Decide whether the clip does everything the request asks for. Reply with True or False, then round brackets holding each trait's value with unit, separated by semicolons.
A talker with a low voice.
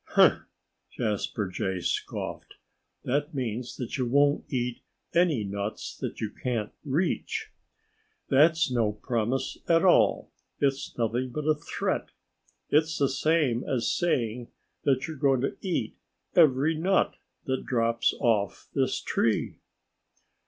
True (130 Hz)